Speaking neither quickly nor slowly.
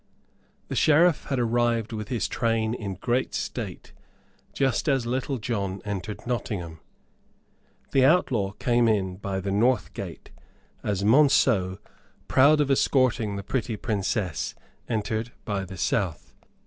No: slow, 130 wpm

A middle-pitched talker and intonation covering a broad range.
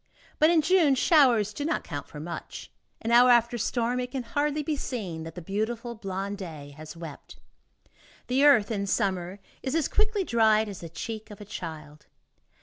No: high, 220 Hz; wide, 6.5 semitones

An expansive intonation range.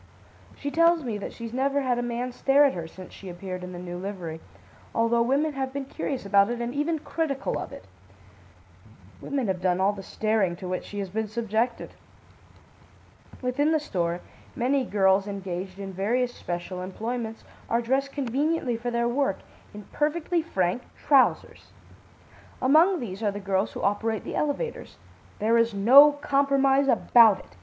Yes: wide, 5.9 semitones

